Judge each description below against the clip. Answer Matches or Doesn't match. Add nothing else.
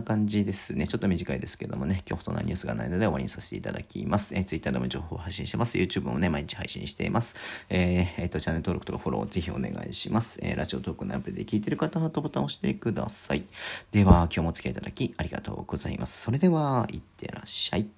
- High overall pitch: Doesn't match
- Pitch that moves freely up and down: Doesn't match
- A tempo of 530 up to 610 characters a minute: Matches